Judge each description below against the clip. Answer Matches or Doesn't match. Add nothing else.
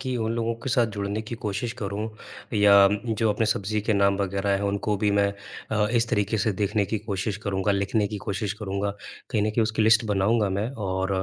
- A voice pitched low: Matches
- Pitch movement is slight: Matches